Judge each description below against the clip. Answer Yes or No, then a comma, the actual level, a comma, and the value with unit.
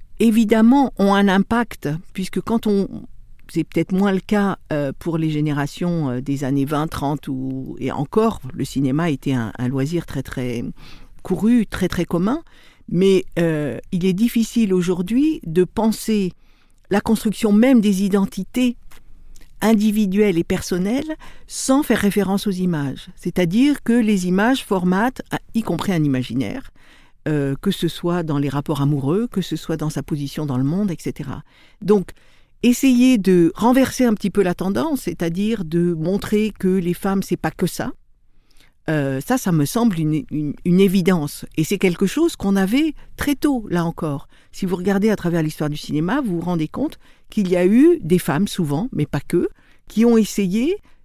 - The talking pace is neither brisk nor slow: Yes, average, 170 wpm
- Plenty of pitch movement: Yes, wide, 5.7 semitones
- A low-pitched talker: No, medium, 185 Hz